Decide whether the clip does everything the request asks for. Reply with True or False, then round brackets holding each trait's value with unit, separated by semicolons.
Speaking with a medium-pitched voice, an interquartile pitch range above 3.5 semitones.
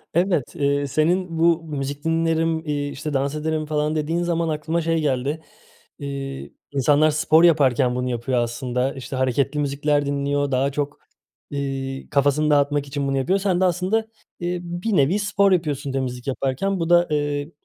False (145 Hz; 3.1 semitones)